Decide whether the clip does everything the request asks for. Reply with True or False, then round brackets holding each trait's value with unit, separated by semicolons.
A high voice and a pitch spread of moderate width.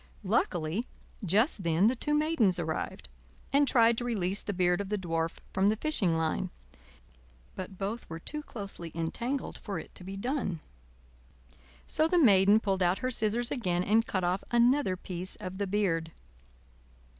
True (200 Hz; 4.8 semitones)